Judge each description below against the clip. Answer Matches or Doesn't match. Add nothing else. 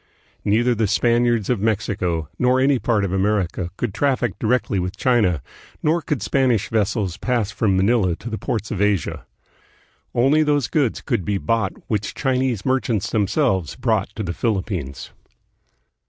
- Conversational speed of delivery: Matches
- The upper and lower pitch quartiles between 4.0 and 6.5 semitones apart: Matches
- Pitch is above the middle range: Doesn't match